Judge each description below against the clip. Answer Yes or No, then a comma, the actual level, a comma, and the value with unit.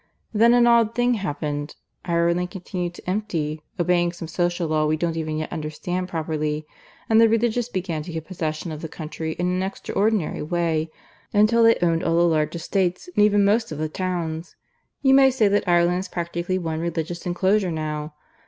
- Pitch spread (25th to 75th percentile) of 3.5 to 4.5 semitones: Yes, average, 3.8 semitones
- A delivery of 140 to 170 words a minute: No, average, 185 wpm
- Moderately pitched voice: Yes, medium, 175 Hz